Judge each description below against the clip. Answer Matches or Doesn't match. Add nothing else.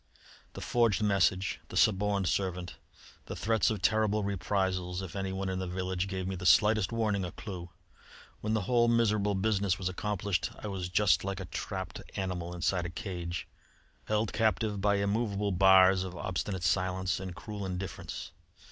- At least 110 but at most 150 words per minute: Doesn't match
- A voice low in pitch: Matches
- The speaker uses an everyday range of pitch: Doesn't match